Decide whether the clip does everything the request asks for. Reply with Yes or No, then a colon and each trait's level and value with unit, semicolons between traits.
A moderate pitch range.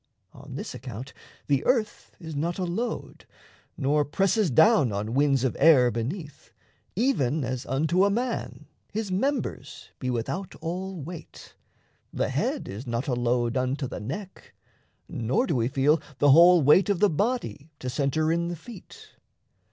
No: wide, 6.6 semitones